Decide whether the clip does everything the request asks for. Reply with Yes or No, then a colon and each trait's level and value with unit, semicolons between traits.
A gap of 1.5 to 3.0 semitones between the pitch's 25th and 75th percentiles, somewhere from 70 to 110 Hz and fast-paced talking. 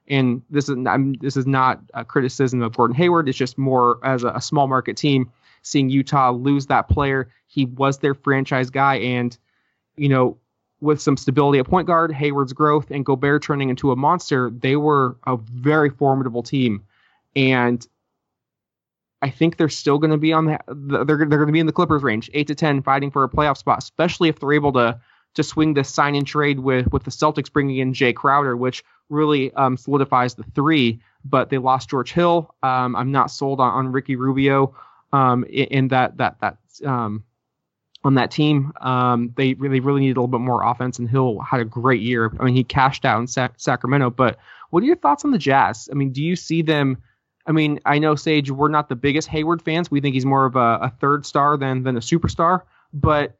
No: narrow, 2.6 semitones; low, 135 Hz; fast, 215 wpm